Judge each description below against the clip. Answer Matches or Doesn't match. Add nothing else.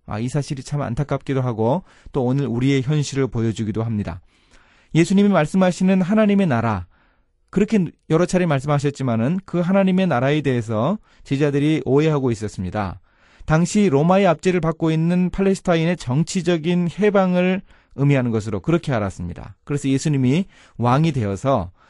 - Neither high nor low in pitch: Matches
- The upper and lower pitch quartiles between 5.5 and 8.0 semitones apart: Matches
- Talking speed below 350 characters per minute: Doesn't match